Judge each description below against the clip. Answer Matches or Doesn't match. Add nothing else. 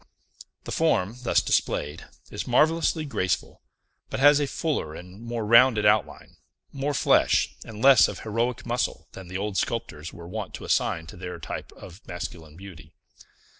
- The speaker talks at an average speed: Matches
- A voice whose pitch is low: Matches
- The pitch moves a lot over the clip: Matches